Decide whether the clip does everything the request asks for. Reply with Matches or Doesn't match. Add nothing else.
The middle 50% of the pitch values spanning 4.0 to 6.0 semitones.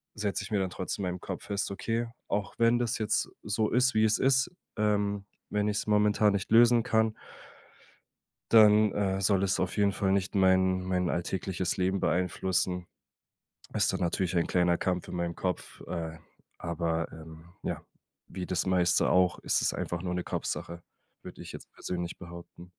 Doesn't match